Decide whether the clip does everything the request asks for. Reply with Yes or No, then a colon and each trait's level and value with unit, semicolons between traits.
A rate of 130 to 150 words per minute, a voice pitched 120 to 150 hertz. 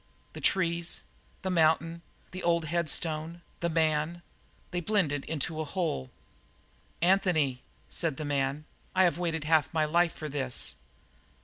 No: slow, 135 wpm; medium, 160 Hz